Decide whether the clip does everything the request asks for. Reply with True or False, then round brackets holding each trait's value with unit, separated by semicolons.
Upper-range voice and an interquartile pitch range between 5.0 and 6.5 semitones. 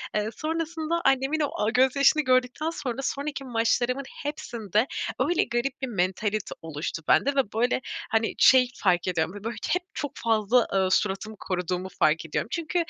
True (245 Hz; 5.3 semitones)